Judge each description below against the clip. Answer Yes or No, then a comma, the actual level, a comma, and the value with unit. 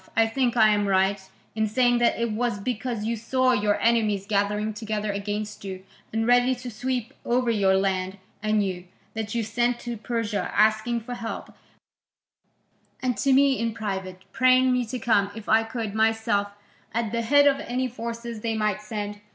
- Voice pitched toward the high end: Yes, high, 225 Hz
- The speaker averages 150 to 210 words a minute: Yes, average, 180 wpm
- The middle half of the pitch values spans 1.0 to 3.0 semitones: Yes, narrow, 2.6 semitones